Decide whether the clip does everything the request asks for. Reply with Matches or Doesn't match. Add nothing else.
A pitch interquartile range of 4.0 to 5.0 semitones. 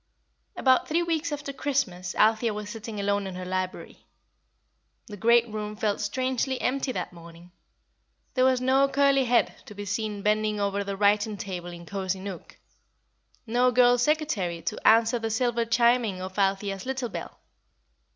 Matches